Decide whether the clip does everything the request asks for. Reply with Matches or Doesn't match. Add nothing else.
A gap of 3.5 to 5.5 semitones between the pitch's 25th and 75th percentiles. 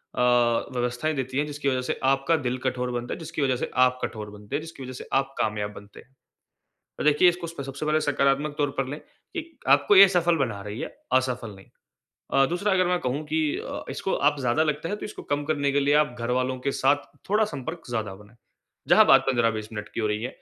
Matches